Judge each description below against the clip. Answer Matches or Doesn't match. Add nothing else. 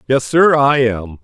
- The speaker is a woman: Doesn't match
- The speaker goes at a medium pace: Matches